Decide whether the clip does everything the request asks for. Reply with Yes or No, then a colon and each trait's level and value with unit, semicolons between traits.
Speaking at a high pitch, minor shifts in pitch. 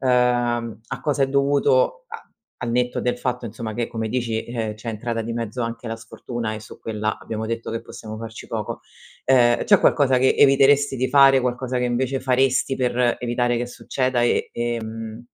No: low, 120 Hz; narrow, 2.2 semitones